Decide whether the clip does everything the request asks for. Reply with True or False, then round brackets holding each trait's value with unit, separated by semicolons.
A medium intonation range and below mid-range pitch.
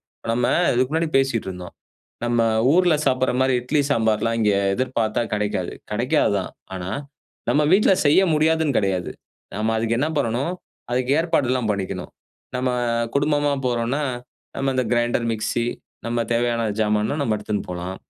True (4.1 semitones; 120 Hz)